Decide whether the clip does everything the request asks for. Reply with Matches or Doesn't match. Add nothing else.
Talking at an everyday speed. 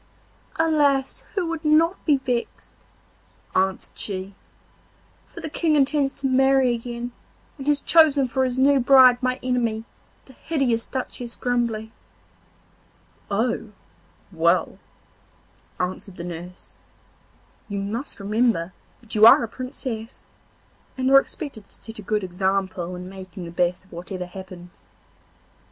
Doesn't match